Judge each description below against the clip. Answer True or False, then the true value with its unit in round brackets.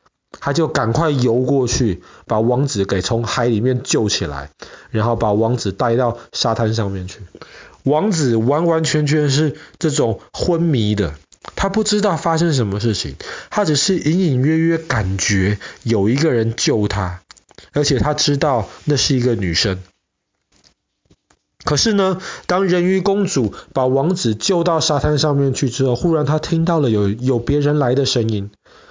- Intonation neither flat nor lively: False (6.1 semitones)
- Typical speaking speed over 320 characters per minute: False (230 characters per minute)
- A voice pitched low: True (130 Hz)